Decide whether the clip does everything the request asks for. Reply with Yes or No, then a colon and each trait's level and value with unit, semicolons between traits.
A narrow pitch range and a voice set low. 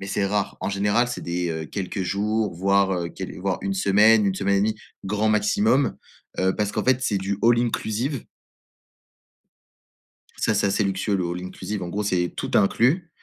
Yes: narrow, 2.2 semitones; low, 100 Hz